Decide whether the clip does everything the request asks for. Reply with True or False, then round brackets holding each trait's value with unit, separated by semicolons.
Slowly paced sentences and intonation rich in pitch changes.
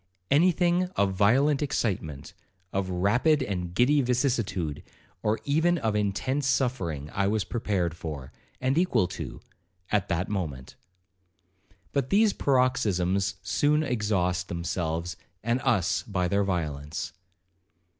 True (120 wpm; 6.9 semitones)